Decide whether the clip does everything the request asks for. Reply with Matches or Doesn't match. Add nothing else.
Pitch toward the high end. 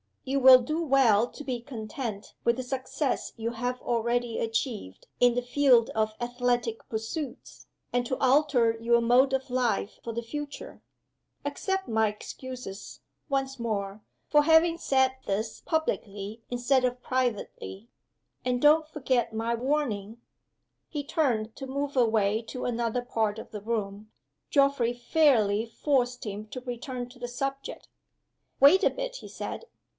Matches